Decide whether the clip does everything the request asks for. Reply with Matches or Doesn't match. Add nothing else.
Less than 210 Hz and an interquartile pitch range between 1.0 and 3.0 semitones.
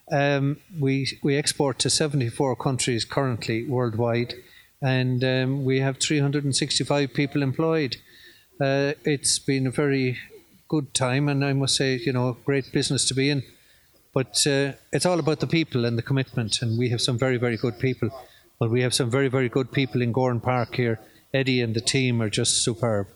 Matches